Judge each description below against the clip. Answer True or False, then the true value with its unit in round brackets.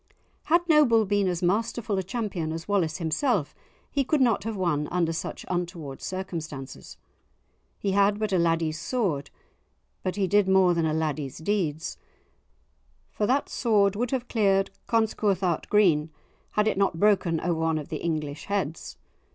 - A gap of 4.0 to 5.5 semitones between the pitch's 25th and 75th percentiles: True (4.5 semitones)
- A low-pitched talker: False (190 Hz)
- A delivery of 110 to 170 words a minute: True (160 wpm)